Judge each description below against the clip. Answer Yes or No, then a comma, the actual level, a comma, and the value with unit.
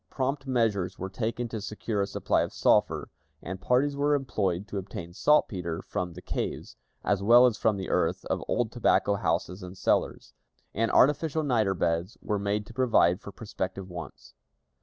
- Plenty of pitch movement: No, average, 4.8 semitones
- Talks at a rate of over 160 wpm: Yes, average, 175 wpm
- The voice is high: No, low, 105 Hz